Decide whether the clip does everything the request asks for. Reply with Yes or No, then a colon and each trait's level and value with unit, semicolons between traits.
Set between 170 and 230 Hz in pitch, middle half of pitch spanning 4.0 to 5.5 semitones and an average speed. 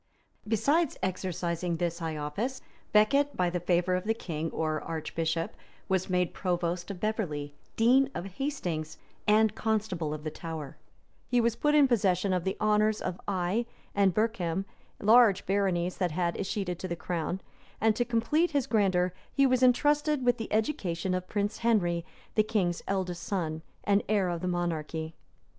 Yes: high, 190 Hz; average, 4.4 semitones; average, 165 wpm